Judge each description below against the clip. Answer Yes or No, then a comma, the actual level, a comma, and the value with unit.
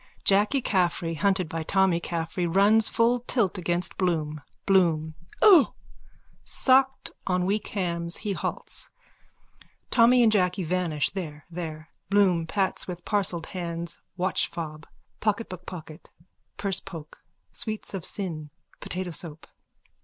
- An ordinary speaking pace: No, slow, 115 wpm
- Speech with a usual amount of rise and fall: Yes, average, 3.4 semitones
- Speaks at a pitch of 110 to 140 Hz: No, medium, 180 Hz